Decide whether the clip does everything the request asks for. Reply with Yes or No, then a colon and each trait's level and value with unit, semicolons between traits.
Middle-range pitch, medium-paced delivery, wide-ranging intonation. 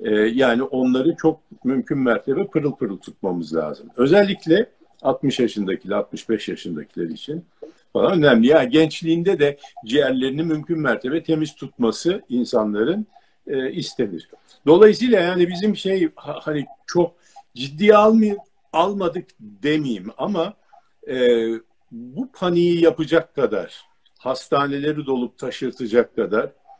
Yes: medium, 165 Hz; average, 105 wpm; wide, 7.8 semitones